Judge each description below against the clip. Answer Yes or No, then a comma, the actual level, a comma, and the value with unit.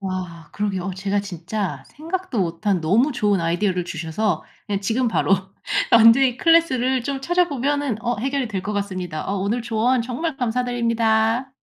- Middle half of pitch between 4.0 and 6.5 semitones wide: Yes, average, 5.1 semitones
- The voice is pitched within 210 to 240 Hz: Yes, high, 220 Hz